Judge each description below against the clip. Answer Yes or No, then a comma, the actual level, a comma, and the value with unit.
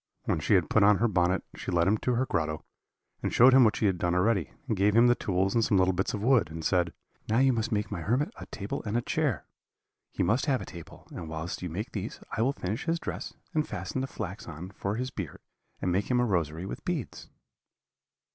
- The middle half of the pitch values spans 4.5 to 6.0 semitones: Yes, average, 5.1 semitones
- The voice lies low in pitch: Yes, low, 105 Hz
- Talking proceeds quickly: Yes, fast, 245 wpm